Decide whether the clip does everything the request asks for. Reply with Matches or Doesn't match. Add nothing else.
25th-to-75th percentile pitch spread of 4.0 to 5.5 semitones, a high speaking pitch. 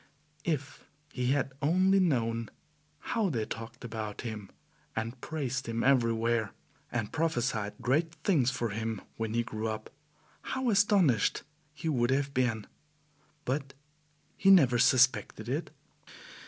Doesn't match